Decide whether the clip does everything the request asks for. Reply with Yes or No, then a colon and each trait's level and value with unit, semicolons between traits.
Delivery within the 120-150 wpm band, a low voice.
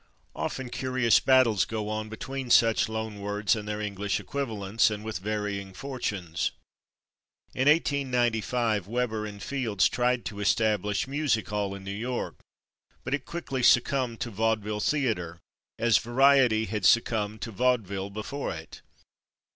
Yes: average, 140 wpm; low, 110 Hz